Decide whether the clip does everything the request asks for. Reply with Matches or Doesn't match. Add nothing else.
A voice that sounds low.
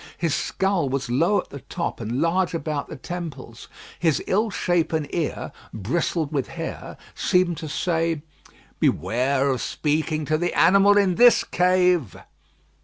Doesn't match